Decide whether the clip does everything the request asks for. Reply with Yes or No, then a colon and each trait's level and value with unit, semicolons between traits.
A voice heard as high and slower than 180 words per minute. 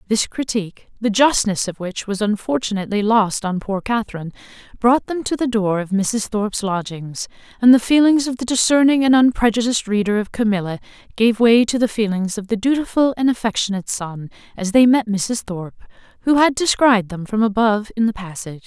No: high, 220 Hz; average, 185 wpm